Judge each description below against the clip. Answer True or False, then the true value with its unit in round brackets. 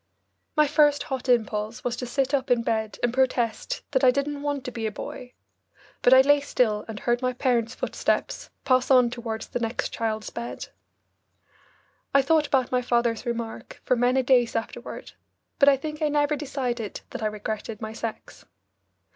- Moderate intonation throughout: True (3.0 semitones)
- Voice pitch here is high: True (250 Hz)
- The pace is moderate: True (180 wpm)